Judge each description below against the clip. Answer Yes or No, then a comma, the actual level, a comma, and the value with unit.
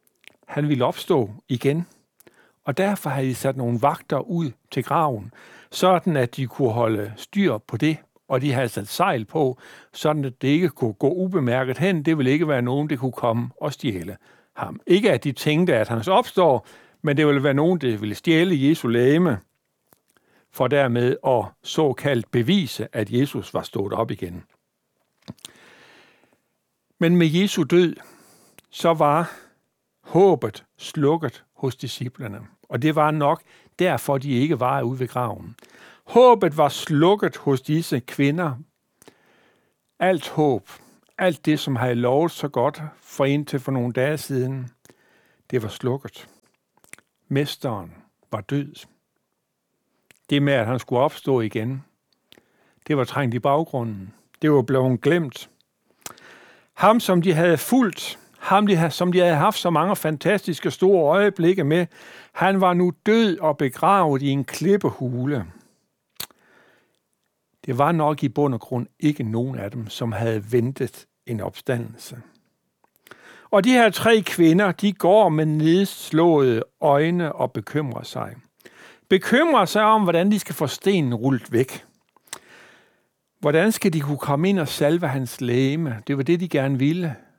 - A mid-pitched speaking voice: Yes, medium, 145 Hz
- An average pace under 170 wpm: Yes, average, 150 wpm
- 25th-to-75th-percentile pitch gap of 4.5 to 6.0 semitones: Yes, average, 5.2 semitones